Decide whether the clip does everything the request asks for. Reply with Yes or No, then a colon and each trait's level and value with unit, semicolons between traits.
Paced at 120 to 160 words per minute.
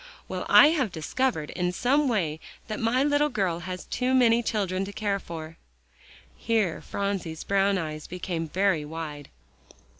Yes: average, 150 wpm